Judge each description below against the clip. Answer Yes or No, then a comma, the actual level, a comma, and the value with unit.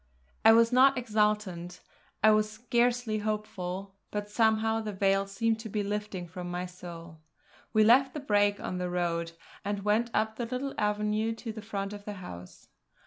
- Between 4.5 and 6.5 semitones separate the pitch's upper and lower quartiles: No, narrow, 2.5 semitones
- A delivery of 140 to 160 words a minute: No, average, 175 wpm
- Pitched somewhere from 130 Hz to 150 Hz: No, high, 210 Hz